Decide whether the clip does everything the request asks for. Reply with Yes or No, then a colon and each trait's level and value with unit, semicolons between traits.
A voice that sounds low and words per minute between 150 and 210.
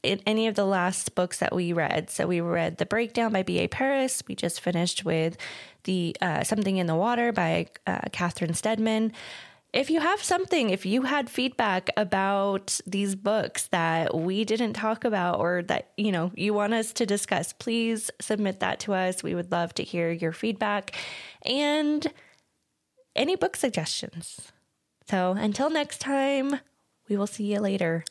No: high, 205 Hz; average, 175 wpm